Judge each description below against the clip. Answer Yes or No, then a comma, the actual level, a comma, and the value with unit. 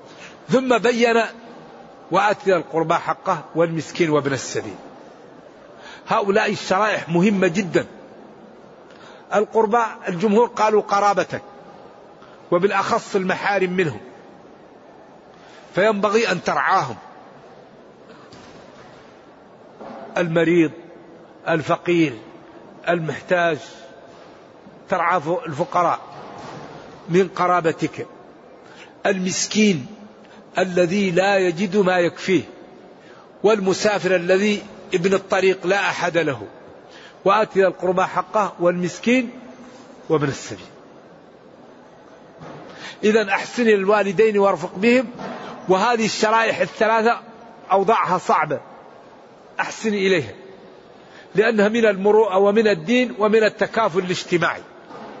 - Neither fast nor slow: Yes, average, 75 wpm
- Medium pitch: No, high, 195 Hz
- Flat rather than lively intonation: No, average, 3.7 semitones